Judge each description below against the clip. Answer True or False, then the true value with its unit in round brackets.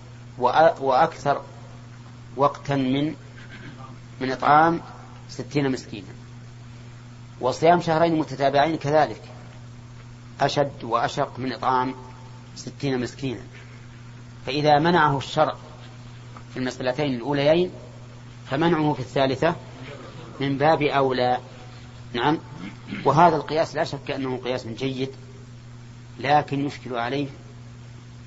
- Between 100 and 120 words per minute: False (85 wpm)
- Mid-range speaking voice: False (125 Hz)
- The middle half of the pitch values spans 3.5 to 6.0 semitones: False (2.7 semitones)